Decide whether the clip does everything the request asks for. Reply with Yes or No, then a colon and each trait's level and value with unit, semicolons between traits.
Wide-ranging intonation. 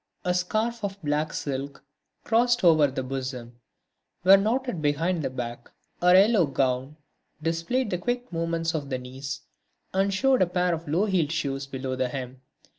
Yes: wide, 6.0 semitones